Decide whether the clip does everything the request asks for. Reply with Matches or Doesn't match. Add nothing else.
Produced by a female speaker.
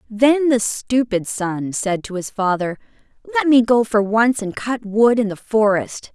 Matches